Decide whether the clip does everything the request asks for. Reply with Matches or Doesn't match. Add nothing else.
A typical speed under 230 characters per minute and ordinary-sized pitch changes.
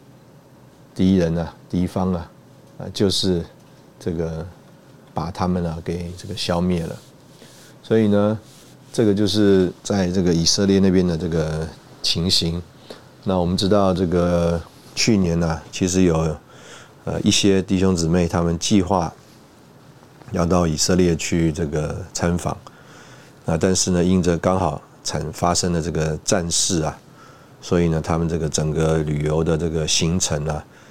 Matches